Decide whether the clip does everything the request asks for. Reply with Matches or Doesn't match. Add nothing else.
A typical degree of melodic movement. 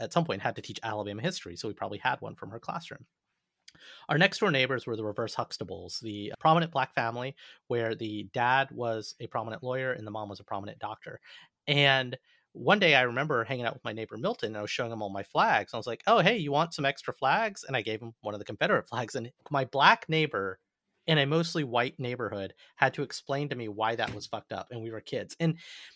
Matches